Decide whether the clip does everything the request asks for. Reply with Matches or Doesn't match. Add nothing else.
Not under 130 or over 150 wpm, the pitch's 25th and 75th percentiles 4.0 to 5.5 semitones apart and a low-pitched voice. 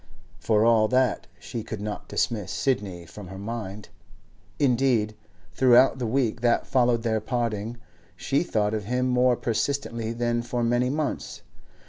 Doesn't match